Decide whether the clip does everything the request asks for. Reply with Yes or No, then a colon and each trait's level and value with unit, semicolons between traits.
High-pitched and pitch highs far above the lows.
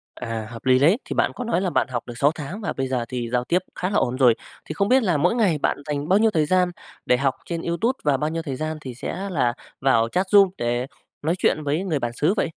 No: medium, 155 Hz; wide, 6.3 semitones